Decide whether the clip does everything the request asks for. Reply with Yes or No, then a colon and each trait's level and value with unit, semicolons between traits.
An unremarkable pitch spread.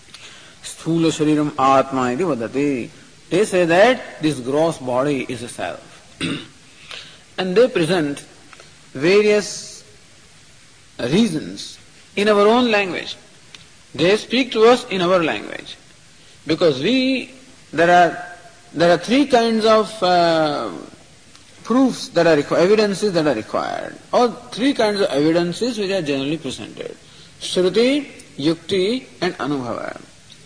No: wide, 6.5 semitones